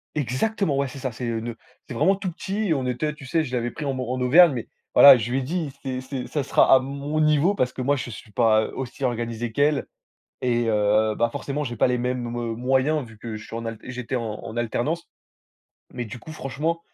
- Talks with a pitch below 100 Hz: No, low, 130 Hz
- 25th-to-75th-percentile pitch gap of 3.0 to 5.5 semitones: Yes, average, 3.7 semitones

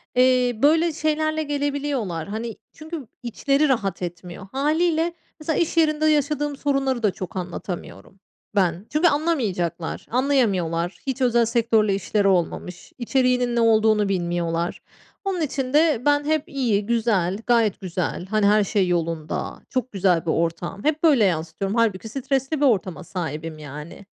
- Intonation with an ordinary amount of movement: No, wide, 7.7 semitones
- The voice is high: Yes, high, 230 Hz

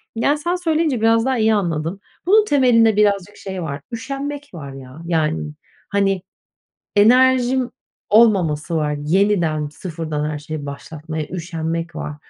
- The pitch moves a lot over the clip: Yes, wide, 7.3 semitones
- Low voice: No, high, 190 Hz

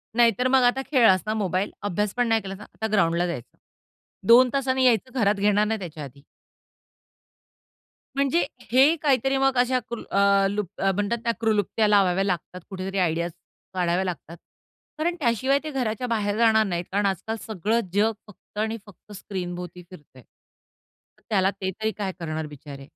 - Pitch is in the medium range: No, high, 205 Hz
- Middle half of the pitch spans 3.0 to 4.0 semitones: No, average, 4.4 semitones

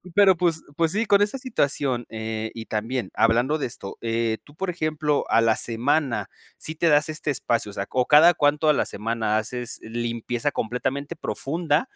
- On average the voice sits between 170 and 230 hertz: No, low, 135 Hz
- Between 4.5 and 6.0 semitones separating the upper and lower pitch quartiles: Yes, wide, 5.4 semitones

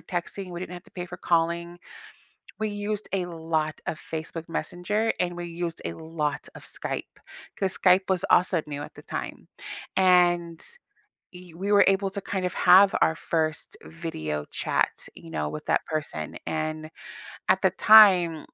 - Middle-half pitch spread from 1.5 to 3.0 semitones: Yes, average, 2.7 semitones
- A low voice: No, medium, 175 Hz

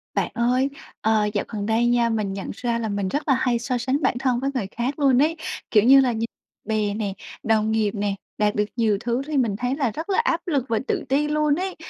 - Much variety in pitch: No, average, 4.0 semitones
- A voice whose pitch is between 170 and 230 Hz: No, high, 240 Hz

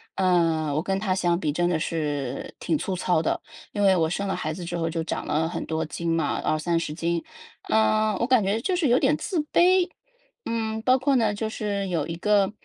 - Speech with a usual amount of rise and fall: Yes, average, 4.9 semitones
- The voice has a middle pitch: Yes, medium, 180 Hz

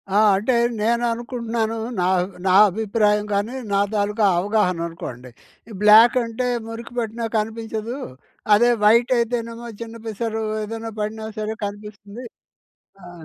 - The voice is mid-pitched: No, high, 220 Hz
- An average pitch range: No, narrow, 2.0 semitones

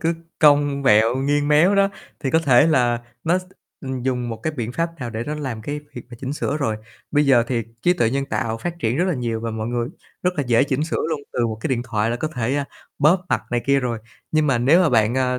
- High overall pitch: No, low, 130 Hz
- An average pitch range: Yes, average, 4.1 semitones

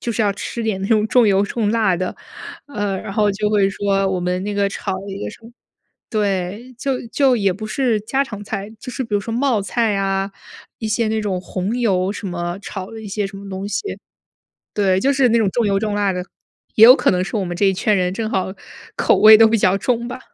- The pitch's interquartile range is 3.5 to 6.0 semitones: No, narrow, 2.6 semitones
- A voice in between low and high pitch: No, high, 205 Hz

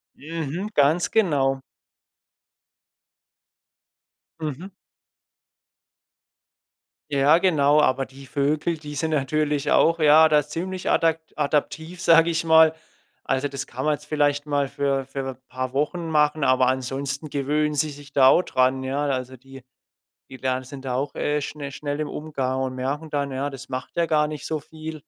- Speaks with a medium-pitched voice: Yes, medium, 145 Hz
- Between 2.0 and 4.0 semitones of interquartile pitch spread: Yes, narrow, 2.5 semitones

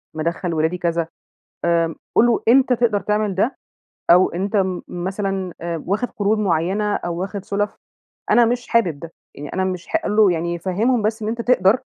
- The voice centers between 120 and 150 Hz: No, high, 195 Hz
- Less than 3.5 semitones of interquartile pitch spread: No, average, 4.0 semitones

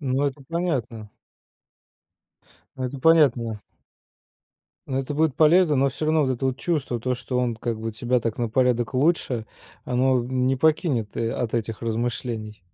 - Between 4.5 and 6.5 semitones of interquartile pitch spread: No, average, 3.4 semitones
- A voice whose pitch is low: Yes, low, 125 Hz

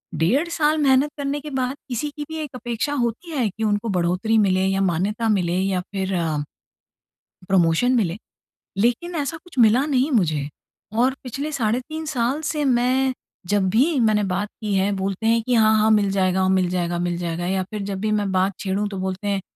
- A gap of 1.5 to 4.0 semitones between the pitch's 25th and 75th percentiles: No, wide, 5.4 semitones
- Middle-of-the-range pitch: No, high, 215 Hz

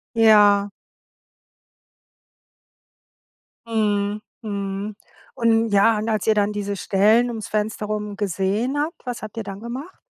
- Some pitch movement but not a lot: No, narrow, 1.9 semitones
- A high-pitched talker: Yes, high, 210 Hz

